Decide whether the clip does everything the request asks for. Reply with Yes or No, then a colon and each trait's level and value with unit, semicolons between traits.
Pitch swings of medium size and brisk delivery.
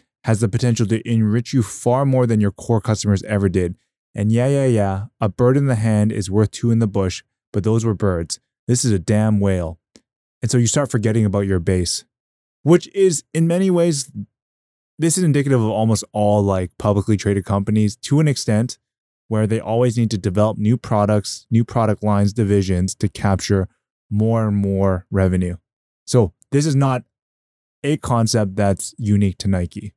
No: average, 3.1 semitones; average, 185 wpm